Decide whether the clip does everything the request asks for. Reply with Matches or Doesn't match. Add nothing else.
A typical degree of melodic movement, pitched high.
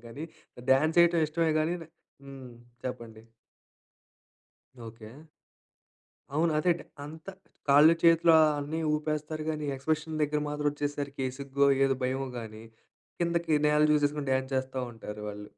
Doesn't match